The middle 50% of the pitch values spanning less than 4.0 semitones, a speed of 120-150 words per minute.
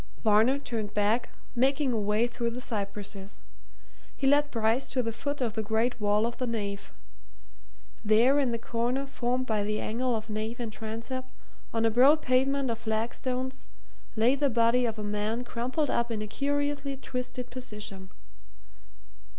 No: average, 3.0 semitones; average, 165 wpm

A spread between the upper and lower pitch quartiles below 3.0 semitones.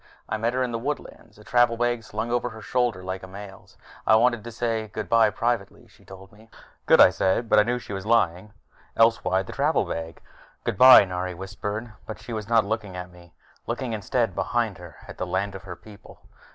No: average, 3.5 semitones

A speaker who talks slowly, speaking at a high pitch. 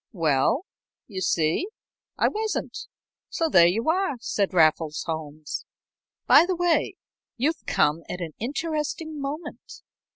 Yes: slow, 125 wpm; high, 230 Hz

